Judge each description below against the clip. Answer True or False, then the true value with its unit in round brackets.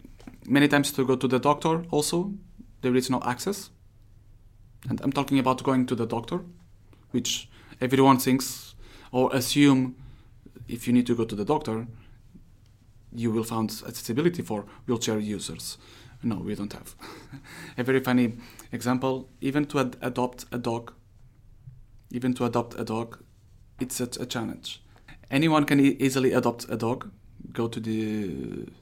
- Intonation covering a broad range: False (3.0 semitones)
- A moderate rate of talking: True (150 wpm)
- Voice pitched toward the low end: True (120 Hz)